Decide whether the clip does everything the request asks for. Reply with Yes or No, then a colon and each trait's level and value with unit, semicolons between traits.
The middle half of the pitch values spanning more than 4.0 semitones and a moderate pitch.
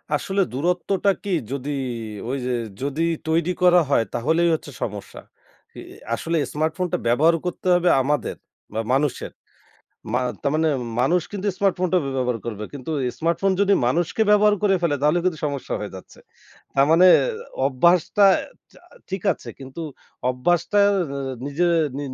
Yes: average, 4.7 semitones; medium, 160 Hz